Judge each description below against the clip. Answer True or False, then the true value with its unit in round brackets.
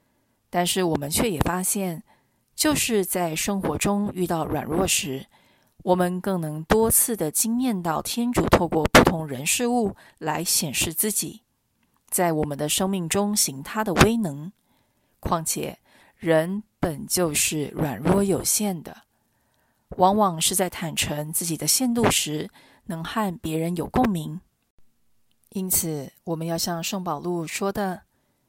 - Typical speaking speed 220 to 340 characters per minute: False (200 characters per minute)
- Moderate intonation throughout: True (4.1 semitones)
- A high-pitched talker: False (175 Hz)